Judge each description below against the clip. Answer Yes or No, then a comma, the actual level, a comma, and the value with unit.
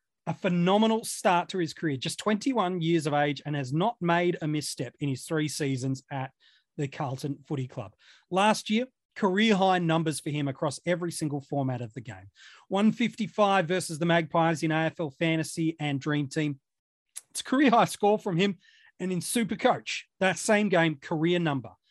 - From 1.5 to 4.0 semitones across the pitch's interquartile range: No, average, 4.6 semitones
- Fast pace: No, average, 180 wpm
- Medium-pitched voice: Yes, medium, 165 Hz